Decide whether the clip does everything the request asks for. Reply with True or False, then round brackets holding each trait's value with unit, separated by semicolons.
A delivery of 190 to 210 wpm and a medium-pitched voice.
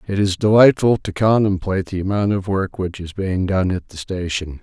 False (205 wpm; 95 Hz)